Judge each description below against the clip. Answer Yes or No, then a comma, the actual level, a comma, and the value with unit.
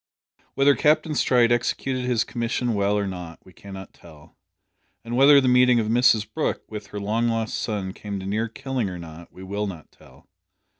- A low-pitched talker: Yes, low, 110 Hz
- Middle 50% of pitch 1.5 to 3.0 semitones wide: No, average, 4.1 semitones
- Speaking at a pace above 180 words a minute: Yes, average, 190 wpm